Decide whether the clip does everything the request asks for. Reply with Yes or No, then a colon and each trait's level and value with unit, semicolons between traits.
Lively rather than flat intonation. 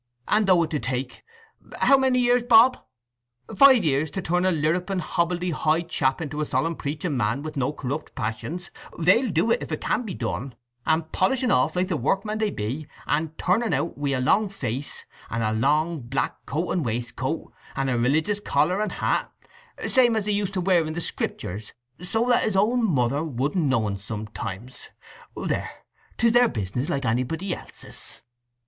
Yes: wide, 7.5 semitones